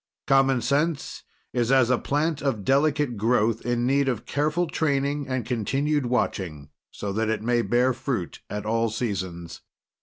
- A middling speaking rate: Yes, average, 155 wpm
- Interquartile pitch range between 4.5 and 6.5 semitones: No, average, 3.9 semitones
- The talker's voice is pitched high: No, low, 125 Hz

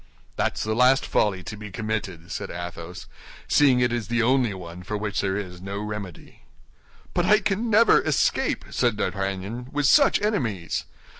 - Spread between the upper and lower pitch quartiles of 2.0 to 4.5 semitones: No, average, 4.9 semitones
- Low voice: Yes, low, 105 Hz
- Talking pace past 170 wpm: No, average, 165 wpm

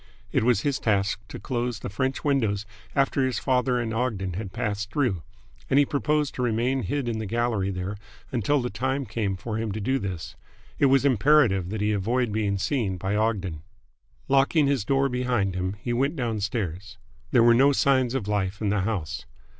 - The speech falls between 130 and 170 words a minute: No, average, 195 wpm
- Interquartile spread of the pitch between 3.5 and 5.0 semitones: Yes, average, 4.6 semitones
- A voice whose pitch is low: Yes, low, 115 Hz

